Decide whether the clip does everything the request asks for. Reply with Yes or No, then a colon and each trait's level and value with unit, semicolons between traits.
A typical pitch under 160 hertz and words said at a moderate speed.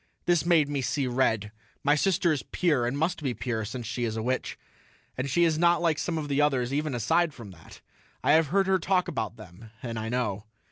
No: low, 135 Hz; fast, 230 wpm